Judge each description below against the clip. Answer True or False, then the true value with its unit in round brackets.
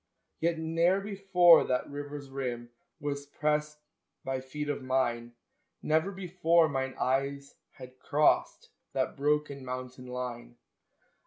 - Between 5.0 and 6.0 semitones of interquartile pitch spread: False (3.7 semitones)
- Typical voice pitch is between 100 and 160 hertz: True (140 Hz)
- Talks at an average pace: False (115 wpm)